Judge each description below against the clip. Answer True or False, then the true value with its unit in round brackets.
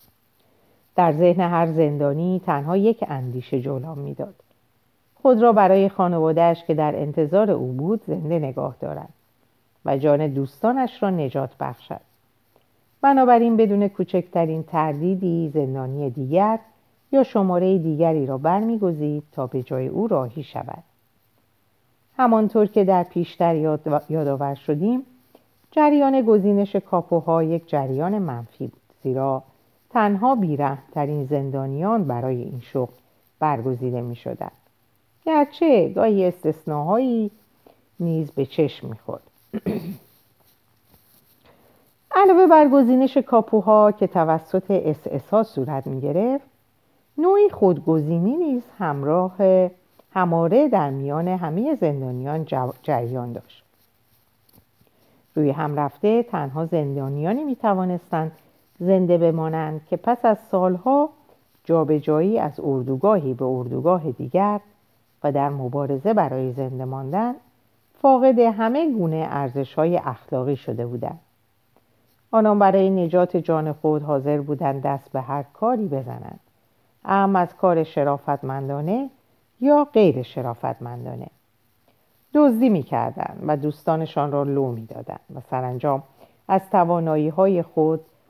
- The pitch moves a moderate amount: False (6.6 semitones)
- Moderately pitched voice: True (160 Hz)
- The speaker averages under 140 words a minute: True (110 wpm)